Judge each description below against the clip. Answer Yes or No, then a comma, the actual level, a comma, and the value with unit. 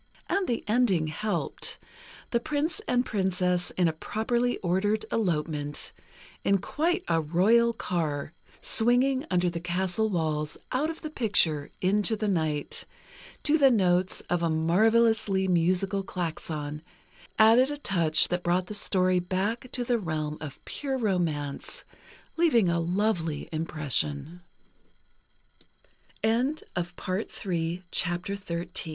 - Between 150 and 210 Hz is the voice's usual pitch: Yes, high, 190 Hz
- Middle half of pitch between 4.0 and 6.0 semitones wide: Yes, wide, 5.6 semitones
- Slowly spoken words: Yes, slow, 115 wpm